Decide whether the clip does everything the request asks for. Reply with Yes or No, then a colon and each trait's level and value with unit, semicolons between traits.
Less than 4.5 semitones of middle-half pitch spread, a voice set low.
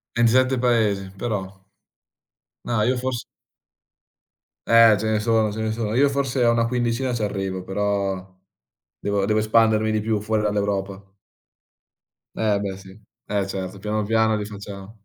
Yes: narrow, 2.5 semitones; low, 105 Hz